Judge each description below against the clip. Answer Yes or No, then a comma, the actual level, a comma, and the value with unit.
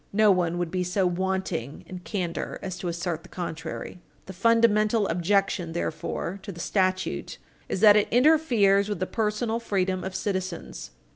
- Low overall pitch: No, high, 190 Hz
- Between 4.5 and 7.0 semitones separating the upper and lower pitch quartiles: No, average, 2.9 semitones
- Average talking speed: Yes, average, 160 wpm